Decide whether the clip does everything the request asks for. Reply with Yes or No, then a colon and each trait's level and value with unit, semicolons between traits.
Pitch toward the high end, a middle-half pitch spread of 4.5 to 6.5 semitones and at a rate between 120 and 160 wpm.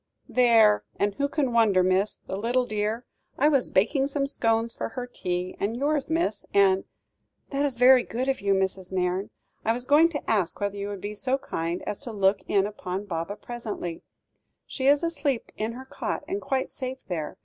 No: high, 225 Hz; average, 5.0 semitones; average, 200 wpm